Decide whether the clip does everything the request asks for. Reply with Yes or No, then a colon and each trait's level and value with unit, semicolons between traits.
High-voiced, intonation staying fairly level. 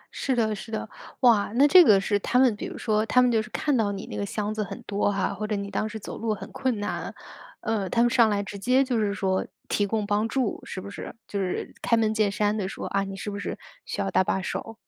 Yes: high, 215 Hz; narrow, 2.2 semitones